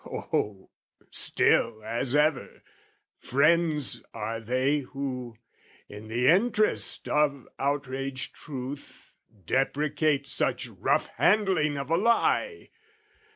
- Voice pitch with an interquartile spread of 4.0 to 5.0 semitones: No, average, 3.4 semitones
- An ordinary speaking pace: No, slow, 95 wpm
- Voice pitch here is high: No, medium, 140 Hz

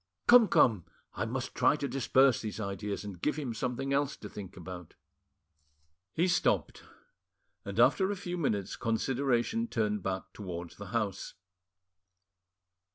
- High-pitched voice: No, low, 115 Hz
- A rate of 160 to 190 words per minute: No, average, 140 wpm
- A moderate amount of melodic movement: No, wide, 6.0 semitones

